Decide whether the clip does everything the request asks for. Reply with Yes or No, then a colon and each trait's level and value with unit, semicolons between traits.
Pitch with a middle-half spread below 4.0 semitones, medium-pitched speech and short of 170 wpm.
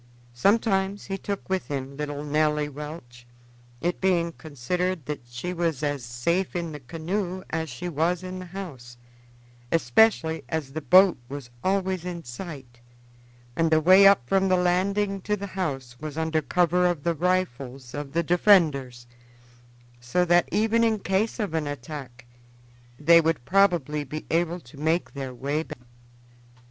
No: average, 4.5 semitones; medium, 165 Hz; average, 155 wpm